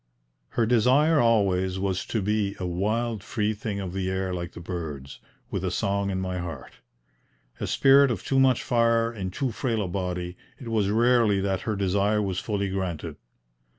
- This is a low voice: Yes, low, 100 Hz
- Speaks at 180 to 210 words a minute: Yes, average, 185 wpm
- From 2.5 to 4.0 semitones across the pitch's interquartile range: Yes, average, 3.7 semitones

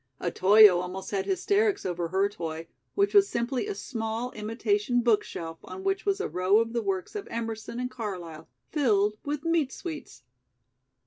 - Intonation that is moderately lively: No, wide, 8.6 semitones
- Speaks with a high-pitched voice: Yes, high, 230 Hz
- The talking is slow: No, average, 170 wpm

